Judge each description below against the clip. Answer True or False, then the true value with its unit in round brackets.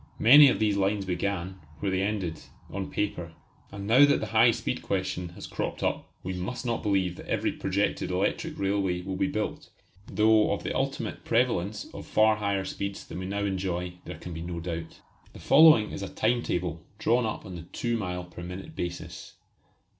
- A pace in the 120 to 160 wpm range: False (195 wpm)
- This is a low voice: True (95 Hz)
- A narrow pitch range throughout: False (3.2 semitones)